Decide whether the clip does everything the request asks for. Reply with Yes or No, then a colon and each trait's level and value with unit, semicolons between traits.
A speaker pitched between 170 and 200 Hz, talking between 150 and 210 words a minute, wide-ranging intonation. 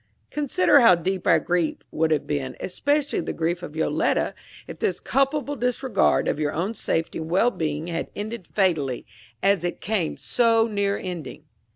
Yes: medium, 185 Hz; average, 170 wpm; wide, 6.0 semitones